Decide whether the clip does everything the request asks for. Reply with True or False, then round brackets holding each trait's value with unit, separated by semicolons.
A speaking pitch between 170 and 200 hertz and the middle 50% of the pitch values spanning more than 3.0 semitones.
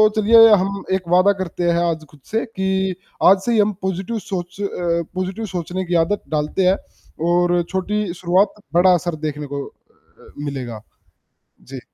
False (185 Hz; 2.4 semitones)